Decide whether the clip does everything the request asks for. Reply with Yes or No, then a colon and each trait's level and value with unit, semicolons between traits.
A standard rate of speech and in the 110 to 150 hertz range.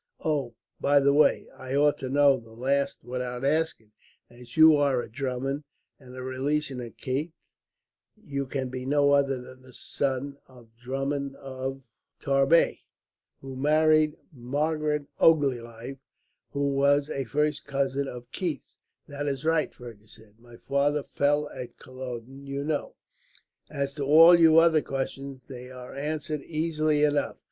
Yes: average, 150 wpm; medium, 140 Hz